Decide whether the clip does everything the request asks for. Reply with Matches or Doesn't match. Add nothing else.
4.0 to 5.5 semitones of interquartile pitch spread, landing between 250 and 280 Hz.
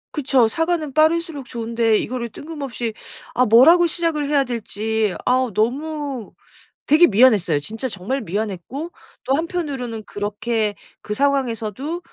Matches